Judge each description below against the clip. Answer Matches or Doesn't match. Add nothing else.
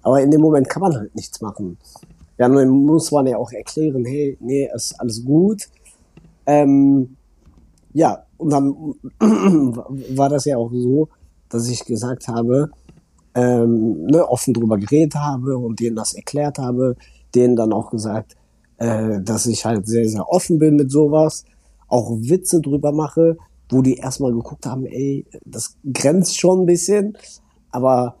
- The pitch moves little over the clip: Doesn't match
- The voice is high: Doesn't match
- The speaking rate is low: Doesn't match